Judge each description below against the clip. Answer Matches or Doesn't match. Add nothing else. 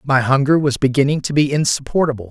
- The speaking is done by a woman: Doesn't match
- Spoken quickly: Doesn't match